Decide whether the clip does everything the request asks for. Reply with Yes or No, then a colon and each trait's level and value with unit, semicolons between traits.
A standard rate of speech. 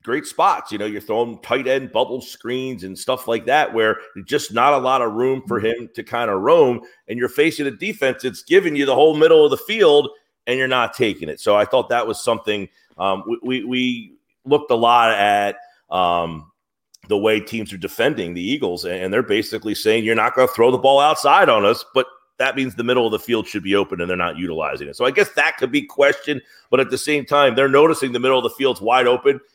No: fast, 240 wpm